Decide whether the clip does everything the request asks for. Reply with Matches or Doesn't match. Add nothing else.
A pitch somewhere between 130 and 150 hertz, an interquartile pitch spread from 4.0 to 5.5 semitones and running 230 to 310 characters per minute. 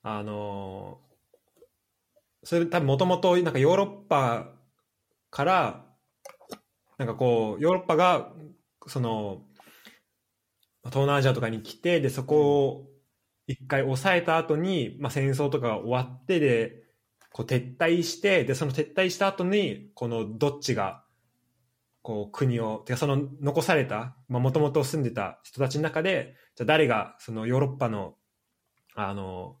Matches